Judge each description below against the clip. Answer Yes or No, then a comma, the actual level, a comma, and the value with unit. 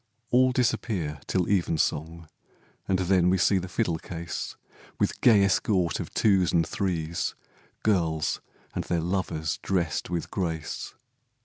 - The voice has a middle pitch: No, very low, 90 Hz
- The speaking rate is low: Yes, slow, 130 wpm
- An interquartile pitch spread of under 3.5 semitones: Yes, average, 3.0 semitones